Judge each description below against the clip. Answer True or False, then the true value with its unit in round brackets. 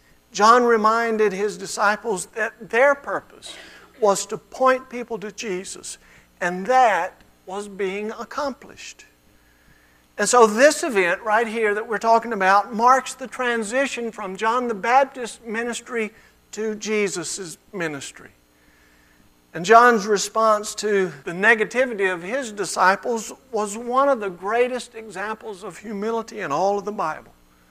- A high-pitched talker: True (215 Hz)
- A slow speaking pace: True (130 wpm)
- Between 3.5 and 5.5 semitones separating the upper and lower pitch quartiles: False (3.1 semitones)